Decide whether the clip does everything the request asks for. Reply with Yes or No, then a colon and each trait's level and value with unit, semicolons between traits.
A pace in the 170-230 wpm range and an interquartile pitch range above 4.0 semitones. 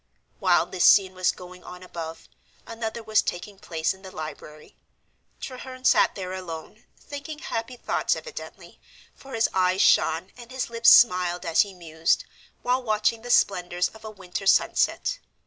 No: average, 160 wpm; average, 4.5 semitones